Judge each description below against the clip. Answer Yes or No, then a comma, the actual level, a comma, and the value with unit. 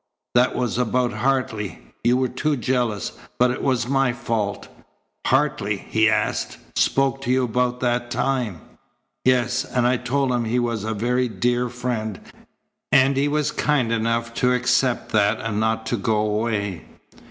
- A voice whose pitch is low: Yes, low, 120 Hz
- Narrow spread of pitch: Yes, narrow, 2.3 semitones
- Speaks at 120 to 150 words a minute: No, average, 160 wpm